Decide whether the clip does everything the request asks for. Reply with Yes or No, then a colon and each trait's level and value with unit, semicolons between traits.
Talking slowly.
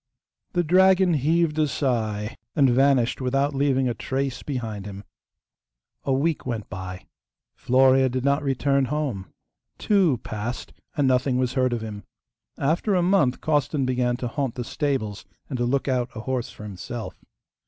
No: average, 160 wpm